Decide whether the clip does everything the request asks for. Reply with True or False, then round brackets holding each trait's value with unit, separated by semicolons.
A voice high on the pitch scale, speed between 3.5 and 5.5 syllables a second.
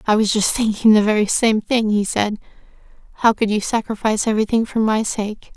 False (215 Hz; 5.7 syllables/s)